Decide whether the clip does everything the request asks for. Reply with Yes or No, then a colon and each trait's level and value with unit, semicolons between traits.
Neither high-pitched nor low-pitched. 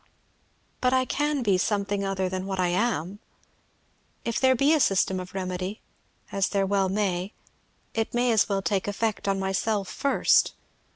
No: high, 200 Hz